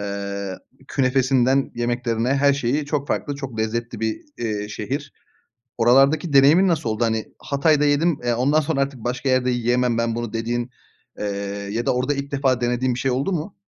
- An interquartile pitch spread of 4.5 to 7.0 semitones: No, average, 3.1 semitones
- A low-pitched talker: Yes, low, 125 Hz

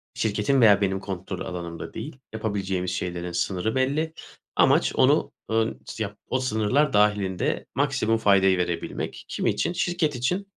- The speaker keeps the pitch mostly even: No, wide, 5.5 semitones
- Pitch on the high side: No, low, 105 Hz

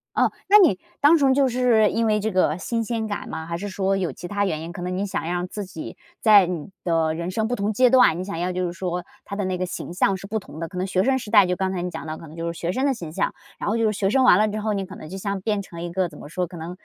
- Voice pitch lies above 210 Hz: No, high, 190 Hz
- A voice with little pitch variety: No, average, 3.6 semitones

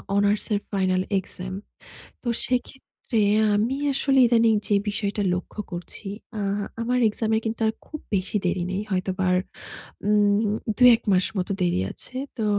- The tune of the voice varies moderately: Yes, average, 3.4 semitones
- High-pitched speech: Yes, high, 205 Hz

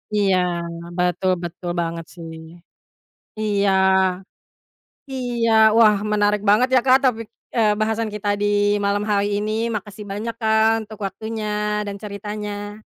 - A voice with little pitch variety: Yes, narrow, 1.5 semitones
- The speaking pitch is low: No, high, 210 Hz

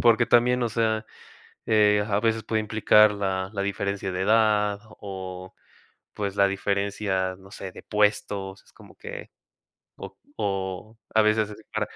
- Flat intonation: Yes, narrow, 2.0 semitones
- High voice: No, low, 105 Hz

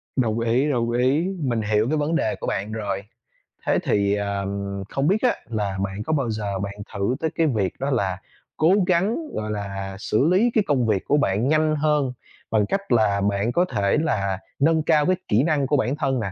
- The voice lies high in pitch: No, low, 120 Hz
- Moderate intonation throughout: No, wide, 6.8 semitones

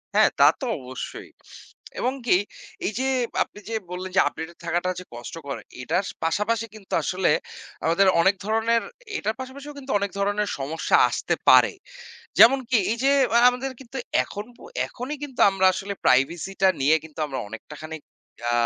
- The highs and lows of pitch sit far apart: Yes, wide, 6.3 semitones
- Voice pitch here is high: Yes, high, 195 Hz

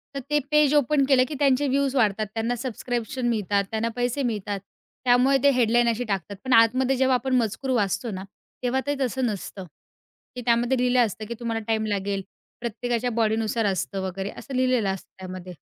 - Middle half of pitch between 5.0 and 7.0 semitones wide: No, average, 3.3 semitones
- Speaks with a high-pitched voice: Yes, high, 235 Hz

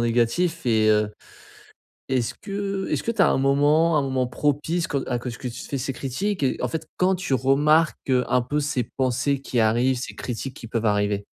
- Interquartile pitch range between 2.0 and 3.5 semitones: No, average, 4.2 semitones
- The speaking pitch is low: Yes, low, 130 Hz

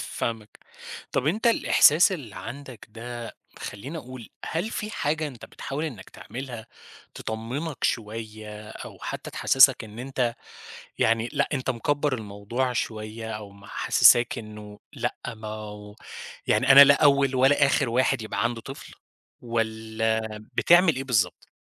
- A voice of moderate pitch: No, low, 120 Hz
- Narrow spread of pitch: No, average, 4.0 semitones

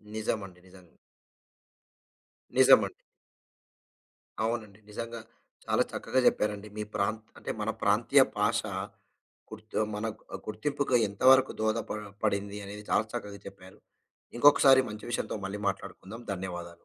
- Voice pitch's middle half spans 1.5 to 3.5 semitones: Yes, narrow, 2.4 semitones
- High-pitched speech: No, low, 105 Hz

